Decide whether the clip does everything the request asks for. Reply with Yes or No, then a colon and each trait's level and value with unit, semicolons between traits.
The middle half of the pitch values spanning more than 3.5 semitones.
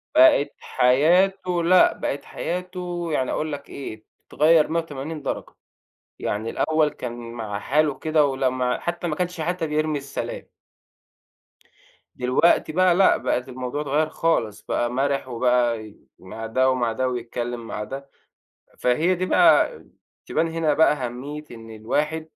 Yes: average, 4.6 semitones